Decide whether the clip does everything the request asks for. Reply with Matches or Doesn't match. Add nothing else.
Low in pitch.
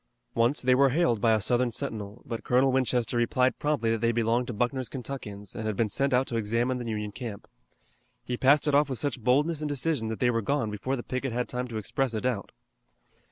Matches